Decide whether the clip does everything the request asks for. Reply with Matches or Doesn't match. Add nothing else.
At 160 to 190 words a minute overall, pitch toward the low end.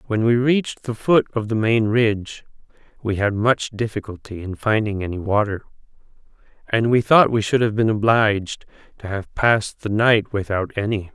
Matches